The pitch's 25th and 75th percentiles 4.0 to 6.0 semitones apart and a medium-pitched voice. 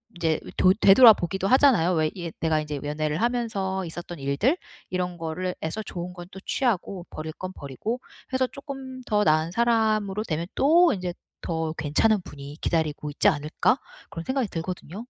Yes: wide, 5.6 semitones; medium, 180 Hz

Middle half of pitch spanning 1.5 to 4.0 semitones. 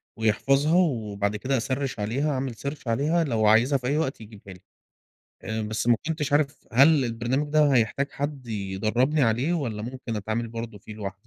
No: average, 4.5 semitones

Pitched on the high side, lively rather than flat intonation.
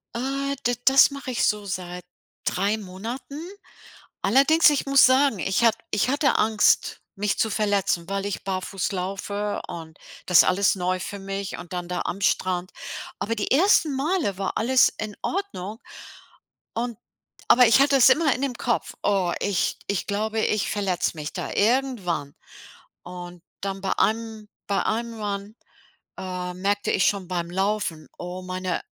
No: high, 205 Hz; average, 4.6 semitones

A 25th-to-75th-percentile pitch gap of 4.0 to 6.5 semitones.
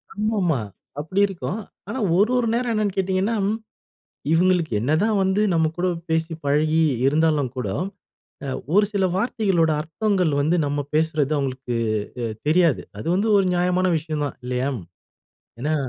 Yes: average, 4.6 semitones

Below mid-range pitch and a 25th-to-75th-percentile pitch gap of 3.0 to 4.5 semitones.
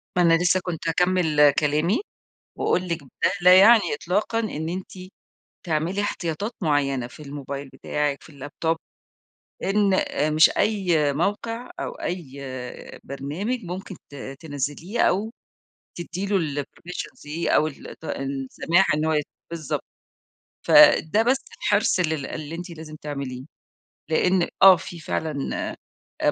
No: medium, 165 Hz; average, 4.2 semitones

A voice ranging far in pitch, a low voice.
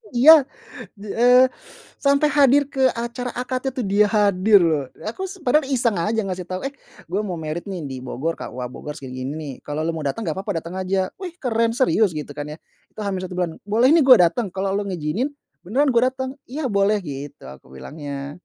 No: wide, 8.0 semitones; high, 200 Hz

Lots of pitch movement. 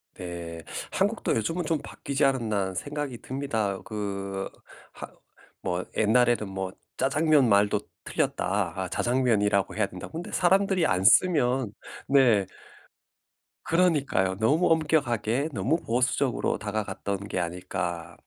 Yes: wide, 6.4 semitones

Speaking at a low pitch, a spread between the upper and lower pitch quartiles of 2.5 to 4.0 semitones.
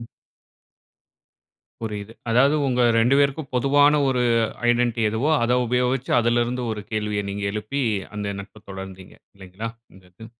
Yes: low, 115 Hz; average, 3.3 semitones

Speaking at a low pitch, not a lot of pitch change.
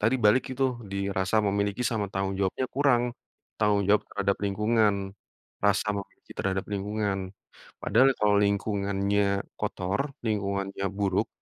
Yes: low, 100 Hz; narrow, 1.5 semitones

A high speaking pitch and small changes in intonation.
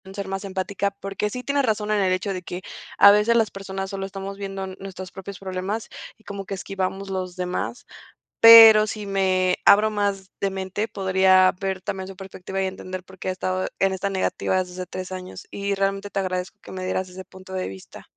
Yes: high, 195 Hz; narrow, 1.3 semitones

